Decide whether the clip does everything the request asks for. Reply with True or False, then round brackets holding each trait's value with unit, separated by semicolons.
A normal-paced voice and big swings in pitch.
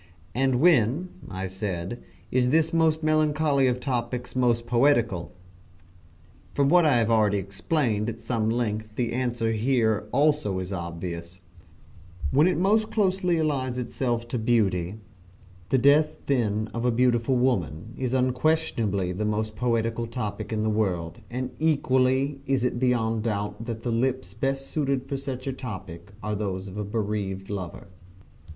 False (150 wpm; 4.2 semitones)